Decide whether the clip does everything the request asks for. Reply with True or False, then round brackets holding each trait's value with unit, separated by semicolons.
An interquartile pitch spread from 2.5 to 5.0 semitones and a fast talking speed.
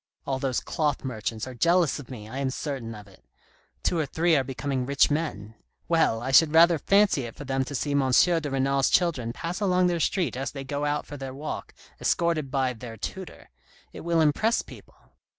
True (4.1 semitones; 210 wpm)